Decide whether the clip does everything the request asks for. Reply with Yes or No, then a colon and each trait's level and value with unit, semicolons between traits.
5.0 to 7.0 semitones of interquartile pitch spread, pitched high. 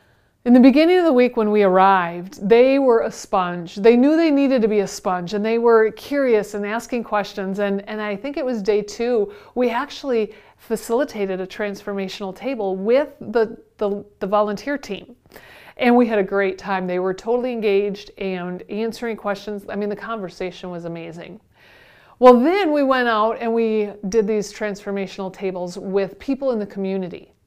No: average, 3.5 semitones; high, 210 Hz